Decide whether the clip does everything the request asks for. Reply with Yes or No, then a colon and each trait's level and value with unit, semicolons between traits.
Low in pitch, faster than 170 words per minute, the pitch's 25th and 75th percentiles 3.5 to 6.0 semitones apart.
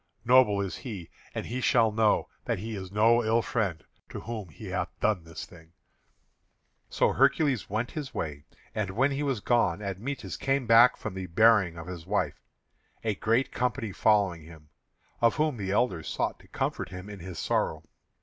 Yes: low, 105 Hz; average, 180 wpm; average, 4.4 semitones